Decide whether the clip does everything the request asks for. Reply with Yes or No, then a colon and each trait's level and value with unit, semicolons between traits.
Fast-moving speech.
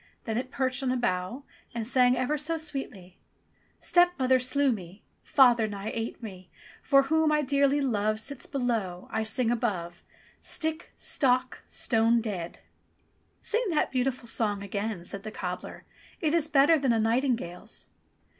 No: average, 155 wpm